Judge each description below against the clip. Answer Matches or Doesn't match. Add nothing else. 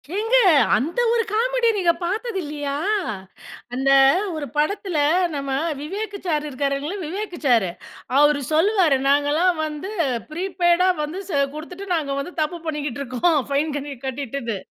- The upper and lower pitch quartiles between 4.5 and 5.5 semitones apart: Matches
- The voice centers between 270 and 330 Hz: Matches